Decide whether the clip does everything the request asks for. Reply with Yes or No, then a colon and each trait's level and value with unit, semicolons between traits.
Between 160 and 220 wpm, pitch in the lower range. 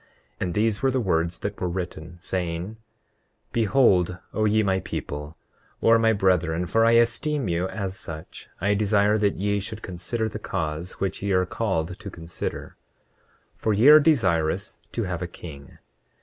Yes: average, 165 wpm; very low, 95 Hz